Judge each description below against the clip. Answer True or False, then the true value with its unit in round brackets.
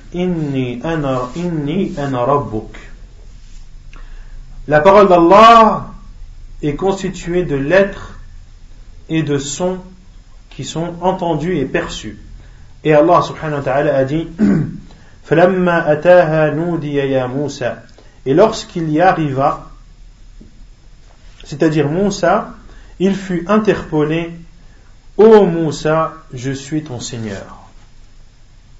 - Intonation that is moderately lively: False (6.2 semitones)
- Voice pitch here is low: False (150 Hz)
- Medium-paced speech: False (90 wpm)